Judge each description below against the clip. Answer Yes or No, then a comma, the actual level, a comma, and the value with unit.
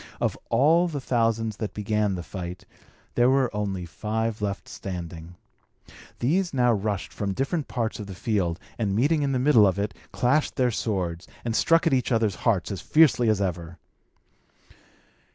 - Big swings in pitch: No, average, 4.7 semitones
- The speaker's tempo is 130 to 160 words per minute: No, average, 170 wpm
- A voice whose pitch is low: Yes, low, 110 Hz